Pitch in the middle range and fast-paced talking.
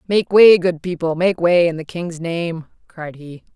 No: medium, 170 Hz; average, 185 wpm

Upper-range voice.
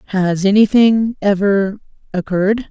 Yes: high, 200 Hz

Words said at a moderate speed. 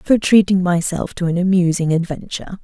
Yes: average, 160 wpm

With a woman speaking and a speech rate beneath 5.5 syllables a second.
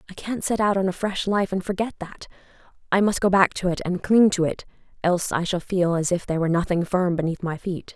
No: female; 6.0 syllables/s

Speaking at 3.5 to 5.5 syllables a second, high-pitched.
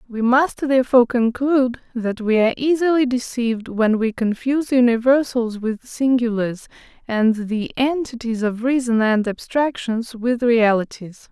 Yes: 4.6 syllables/s; high, 240 Hz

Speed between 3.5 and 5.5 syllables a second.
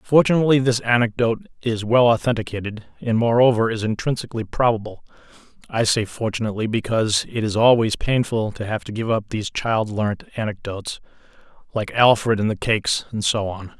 No: 5.8 syllables/s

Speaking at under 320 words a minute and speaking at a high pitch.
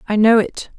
Yes: fast, 230 wpm; high, 220 Hz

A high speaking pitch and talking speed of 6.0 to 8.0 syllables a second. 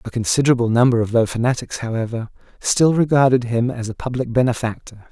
No: low, 120 Hz; 6.2 syllables/s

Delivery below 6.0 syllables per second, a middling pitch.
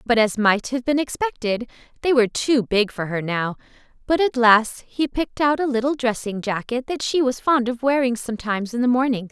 No: 5.4 syllables/s; high, 245 Hz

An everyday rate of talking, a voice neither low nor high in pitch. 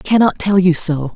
No: fast, 260 wpm; medium, 180 Hz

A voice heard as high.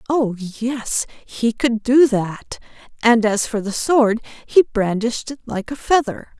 Yes: high, 235 Hz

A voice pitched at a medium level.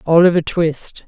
Yes: medium, 165 Hz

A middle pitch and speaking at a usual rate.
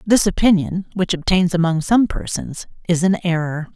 Yes: medium, 180 Hz; average, 160 wpm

